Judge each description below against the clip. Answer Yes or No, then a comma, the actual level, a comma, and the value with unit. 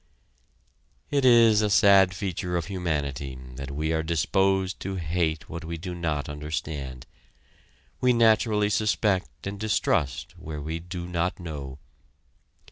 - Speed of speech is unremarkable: No, slow, 130 wpm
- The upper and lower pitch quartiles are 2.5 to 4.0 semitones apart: No, average, 4.4 semitones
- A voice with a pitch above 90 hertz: No, very low, 85 Hz